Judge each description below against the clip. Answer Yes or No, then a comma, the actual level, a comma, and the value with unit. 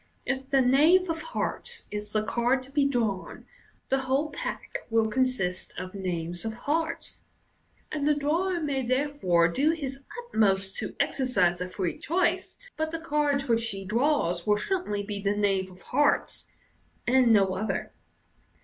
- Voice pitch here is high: Yes, very high, 255 Hz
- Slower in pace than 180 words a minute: Yes, average, 160 wpm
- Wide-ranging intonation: Yes, wide, 6.6 semitones